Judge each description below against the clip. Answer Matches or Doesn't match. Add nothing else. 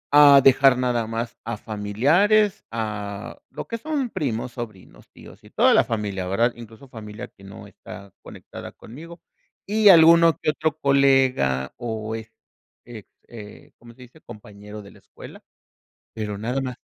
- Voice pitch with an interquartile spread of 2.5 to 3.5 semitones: Doesn't match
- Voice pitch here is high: Doesn't match